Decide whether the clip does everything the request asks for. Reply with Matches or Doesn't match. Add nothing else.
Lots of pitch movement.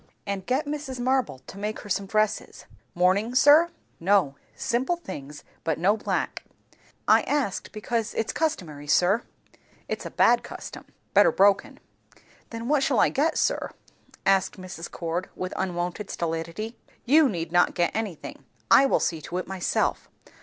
Matches